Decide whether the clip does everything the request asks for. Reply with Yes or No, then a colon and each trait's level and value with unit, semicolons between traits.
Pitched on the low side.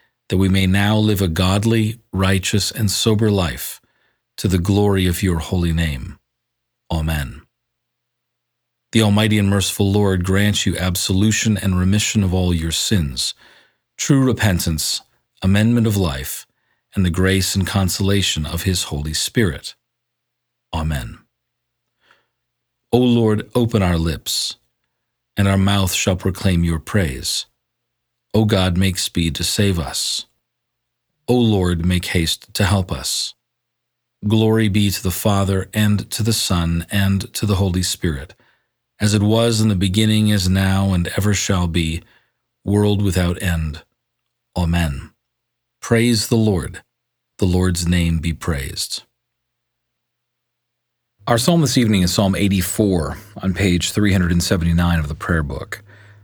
Yes: very low, 95 Hz